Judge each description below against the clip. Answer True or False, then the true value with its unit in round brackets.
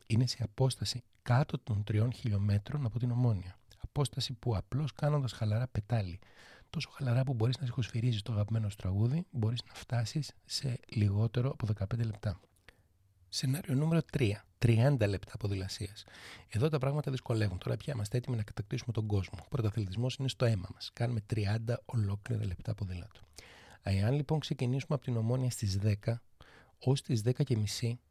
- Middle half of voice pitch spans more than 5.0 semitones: False (3.6 semitones)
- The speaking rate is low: False (155 wpm)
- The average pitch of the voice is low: True (115 Hz)